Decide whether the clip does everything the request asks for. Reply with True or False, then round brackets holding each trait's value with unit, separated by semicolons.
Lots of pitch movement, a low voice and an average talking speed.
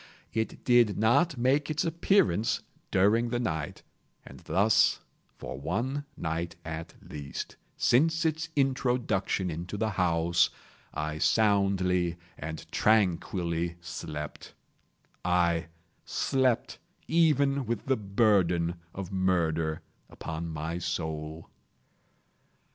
False (6.4 semitones; 95 Hz; 100 wpm)